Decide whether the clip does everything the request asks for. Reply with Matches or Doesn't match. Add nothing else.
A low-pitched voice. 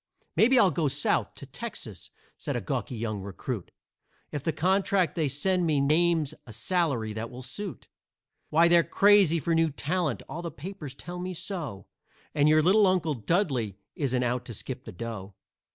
Doesn't match